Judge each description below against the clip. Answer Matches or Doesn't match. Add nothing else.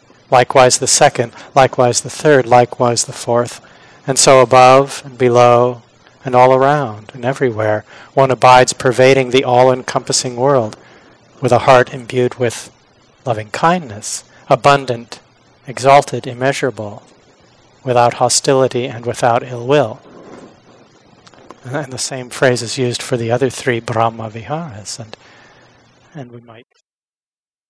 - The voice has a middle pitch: Doesn't match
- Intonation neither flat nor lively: Doesn't match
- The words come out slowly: Matches